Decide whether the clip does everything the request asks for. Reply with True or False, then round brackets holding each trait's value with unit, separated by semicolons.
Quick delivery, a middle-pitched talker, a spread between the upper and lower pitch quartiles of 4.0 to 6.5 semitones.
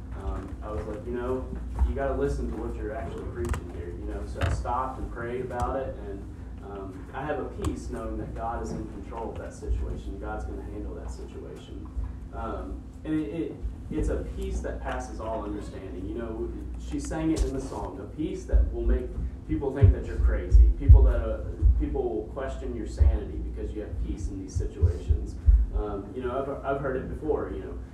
False (215 wpm; 95 Hz; 4.3 semitones)